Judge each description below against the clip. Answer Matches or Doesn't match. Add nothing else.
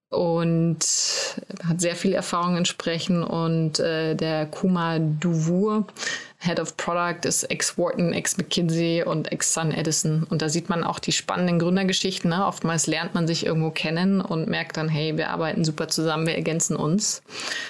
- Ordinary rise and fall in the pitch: Doesn't match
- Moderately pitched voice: Matches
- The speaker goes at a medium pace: Matches